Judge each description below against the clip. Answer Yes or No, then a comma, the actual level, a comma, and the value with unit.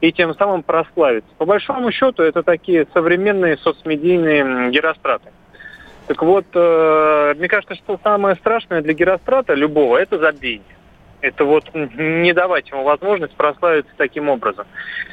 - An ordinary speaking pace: Yes, average, 130 wpm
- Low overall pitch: No, medium, 170 Hz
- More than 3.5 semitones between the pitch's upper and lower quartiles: Yes, average, 4.1 semitones